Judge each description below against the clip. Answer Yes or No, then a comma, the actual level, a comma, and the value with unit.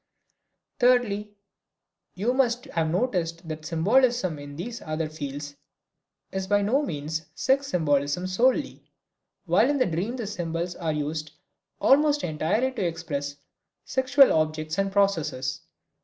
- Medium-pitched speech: Yes, medium, 175 Hz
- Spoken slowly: Yes, slow, 125 wpm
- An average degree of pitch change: No, wide, 7.6 semitones